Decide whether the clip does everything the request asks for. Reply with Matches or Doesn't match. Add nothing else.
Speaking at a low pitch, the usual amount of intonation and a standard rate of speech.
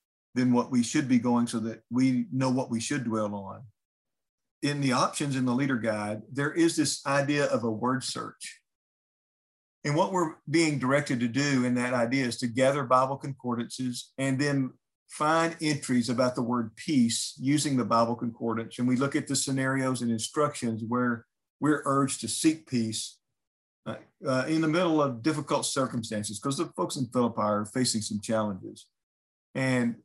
Matches